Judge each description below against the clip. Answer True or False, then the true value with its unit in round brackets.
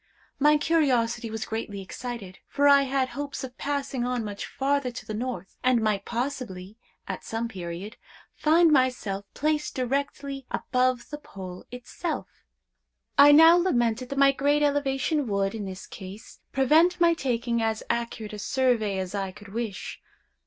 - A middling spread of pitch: True (4.7 semitones)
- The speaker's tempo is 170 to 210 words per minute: False (155 wpm)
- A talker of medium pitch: False (250 Hz)